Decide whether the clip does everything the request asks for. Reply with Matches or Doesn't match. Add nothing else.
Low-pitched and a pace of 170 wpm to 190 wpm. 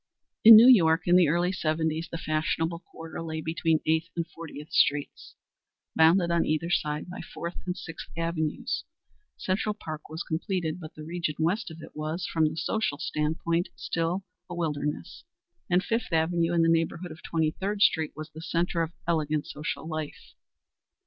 Doesn't match